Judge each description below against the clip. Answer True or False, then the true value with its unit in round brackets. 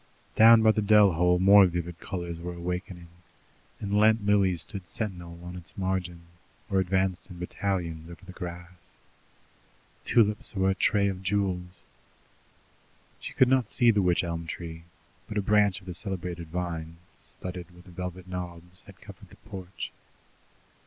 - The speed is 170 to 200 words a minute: False (155 wpm)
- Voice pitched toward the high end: False (90 Hz)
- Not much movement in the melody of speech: True (2.3 semitones)